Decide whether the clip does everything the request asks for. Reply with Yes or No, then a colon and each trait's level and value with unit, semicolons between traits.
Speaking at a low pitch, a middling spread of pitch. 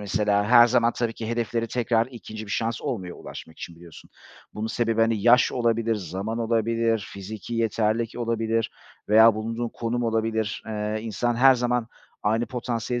No: low, 115 Hz; narrow, 1.5 semitones